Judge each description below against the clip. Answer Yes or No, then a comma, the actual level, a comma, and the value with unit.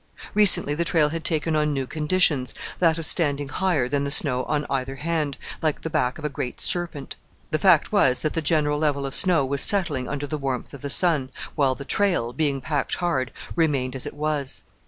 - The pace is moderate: No, fast, 210 wpm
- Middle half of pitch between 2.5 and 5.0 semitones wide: Yes, average, 3.0 semitones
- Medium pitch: Yes, medium, 150 Hz